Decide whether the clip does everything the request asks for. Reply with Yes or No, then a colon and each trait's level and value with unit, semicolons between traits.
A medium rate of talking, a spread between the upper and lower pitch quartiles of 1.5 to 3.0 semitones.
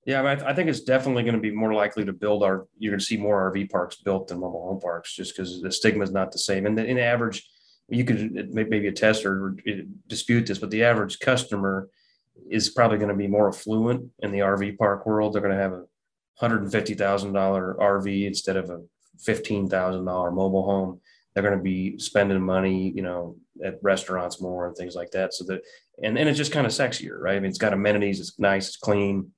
No: fast, 235 wpm; narrow, 2.4 semitones